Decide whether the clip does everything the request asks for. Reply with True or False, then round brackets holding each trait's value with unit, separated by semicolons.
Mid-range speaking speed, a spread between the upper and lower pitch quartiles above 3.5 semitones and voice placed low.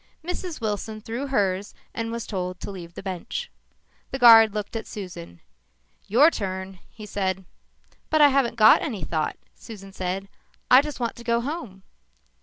False (165 wpm; 4.1 semitones; 215 Hz)